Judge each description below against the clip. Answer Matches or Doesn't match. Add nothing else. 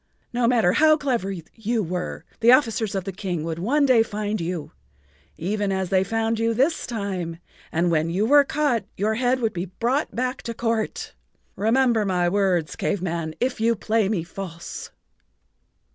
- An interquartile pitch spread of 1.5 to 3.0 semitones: Doesn't match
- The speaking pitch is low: Doesn't match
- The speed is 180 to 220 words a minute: Doesn't match